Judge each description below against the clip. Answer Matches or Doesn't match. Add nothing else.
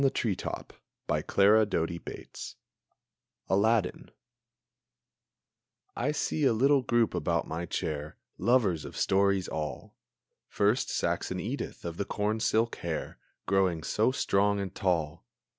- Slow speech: Matches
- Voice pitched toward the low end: Matches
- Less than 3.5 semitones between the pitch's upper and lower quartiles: Doesn't match